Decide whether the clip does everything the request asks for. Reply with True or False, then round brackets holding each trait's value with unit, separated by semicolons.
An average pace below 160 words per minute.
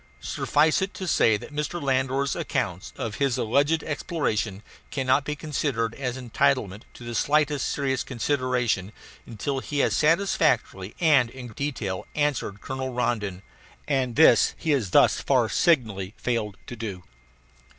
True (140 wpm)